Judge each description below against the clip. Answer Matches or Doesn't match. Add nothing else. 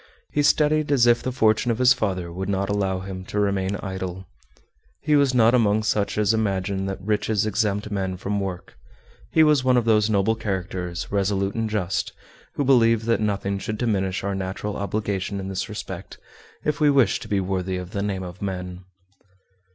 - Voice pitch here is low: Matches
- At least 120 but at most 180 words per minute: Doesn't match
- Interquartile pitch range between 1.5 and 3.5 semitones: Matches